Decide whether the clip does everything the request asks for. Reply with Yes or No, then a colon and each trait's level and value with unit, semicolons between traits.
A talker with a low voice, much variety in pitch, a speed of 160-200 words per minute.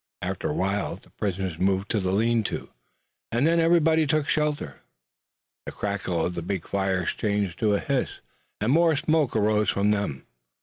Yes: low, 105 Hz; wide, 7.1 semitones; average, 175 wpm